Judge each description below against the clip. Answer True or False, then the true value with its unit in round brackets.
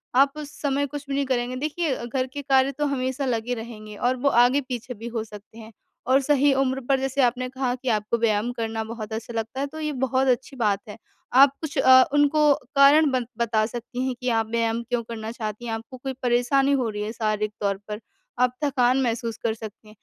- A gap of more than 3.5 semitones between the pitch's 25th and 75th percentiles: False (3.1 semitones)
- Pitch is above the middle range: True (245 Hz)